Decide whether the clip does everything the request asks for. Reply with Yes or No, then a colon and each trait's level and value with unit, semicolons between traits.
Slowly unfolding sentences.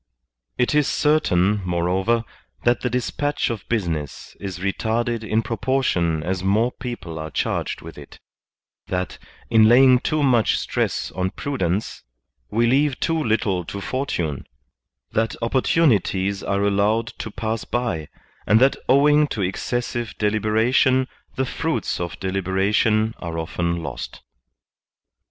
Yes: slow, 130 wpm